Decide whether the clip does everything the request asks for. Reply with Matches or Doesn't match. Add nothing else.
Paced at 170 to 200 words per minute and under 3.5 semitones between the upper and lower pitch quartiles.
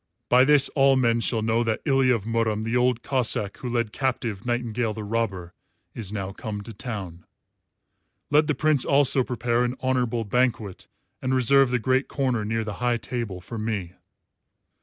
Matches